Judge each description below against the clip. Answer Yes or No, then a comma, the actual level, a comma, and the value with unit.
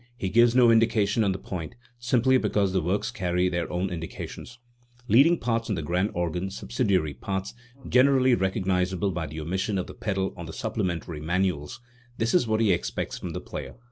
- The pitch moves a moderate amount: Yes, average, 4.3 semitones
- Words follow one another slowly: No, average, 185 wpm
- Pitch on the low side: Yes, very low, 95 Hz